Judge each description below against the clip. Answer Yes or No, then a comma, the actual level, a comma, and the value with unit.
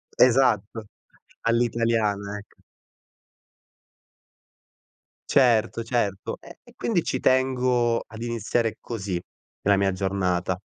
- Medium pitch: No, low, 115 Hz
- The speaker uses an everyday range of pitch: Yes, average, 3.2 semitones